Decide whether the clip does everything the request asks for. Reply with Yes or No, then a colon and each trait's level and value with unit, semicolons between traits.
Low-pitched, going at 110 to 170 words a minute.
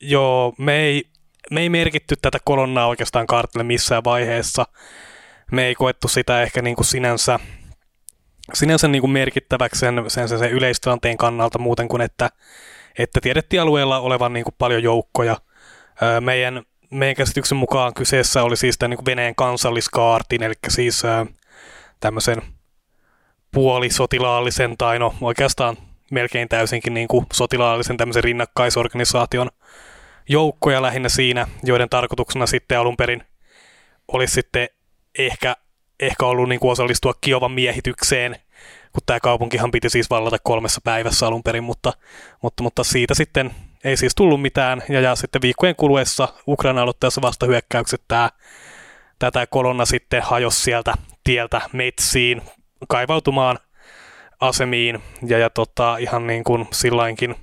Yes: low, 125 Hz; average, 135 wpm